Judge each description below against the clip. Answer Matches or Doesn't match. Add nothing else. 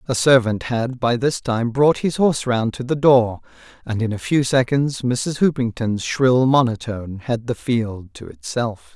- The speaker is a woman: Doesn't match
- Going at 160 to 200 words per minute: Matches